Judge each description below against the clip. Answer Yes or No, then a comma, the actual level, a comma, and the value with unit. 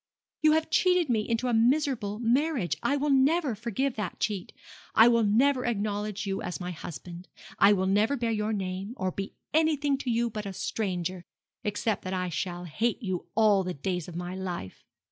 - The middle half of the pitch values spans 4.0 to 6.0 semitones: Yes, average, 5.0 semitones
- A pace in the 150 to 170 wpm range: No, average, 190 wpm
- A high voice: Yes, high, 210 Hz